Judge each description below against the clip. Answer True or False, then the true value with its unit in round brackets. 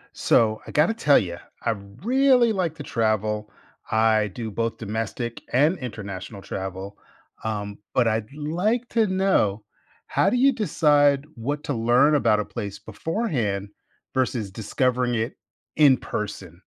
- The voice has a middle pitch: False (115 Hz)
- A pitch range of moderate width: False (6.1 semitones)